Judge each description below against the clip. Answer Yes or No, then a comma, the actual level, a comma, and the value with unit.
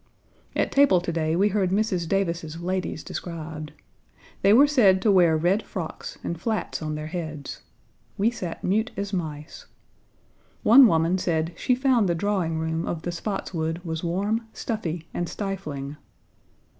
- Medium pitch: Yes, medium, 175 Hz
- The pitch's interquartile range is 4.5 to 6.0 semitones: No, average, 4.0 semitones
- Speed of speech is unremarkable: Yes, average, 155 wpm